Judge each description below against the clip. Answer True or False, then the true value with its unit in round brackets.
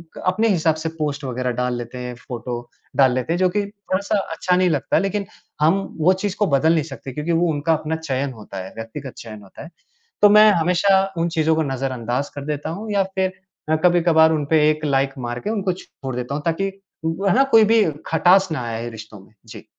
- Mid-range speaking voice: True (155 Hz)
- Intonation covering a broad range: True (6.0 semitones)